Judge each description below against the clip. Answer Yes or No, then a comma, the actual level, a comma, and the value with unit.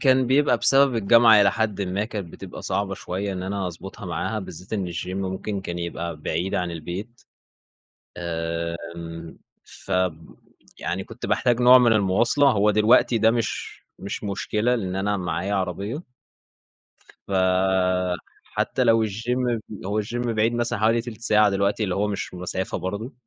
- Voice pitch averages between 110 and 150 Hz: No, low, 100 Hz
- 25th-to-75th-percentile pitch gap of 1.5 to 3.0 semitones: No, average, 3.7 semitones